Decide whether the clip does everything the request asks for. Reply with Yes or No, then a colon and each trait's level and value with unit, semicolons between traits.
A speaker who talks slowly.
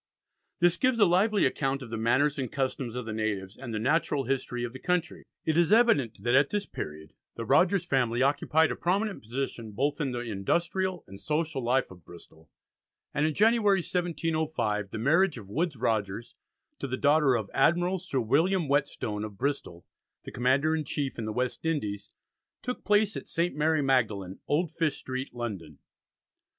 No: average, 180 wpm